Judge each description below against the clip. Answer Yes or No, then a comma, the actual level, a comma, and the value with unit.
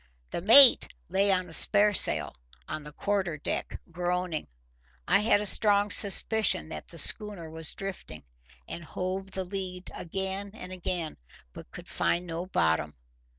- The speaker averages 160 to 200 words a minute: No, average, 150 wpm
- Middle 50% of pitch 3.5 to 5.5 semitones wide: No, average, 3.0 semitones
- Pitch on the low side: No, medium, 185 Hz